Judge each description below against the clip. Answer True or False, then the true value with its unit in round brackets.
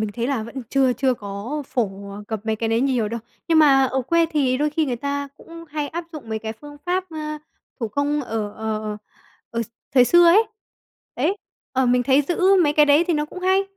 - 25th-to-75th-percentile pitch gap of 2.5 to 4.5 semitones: False (5.1 semitones)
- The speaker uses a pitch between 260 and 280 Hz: True (270 Hz)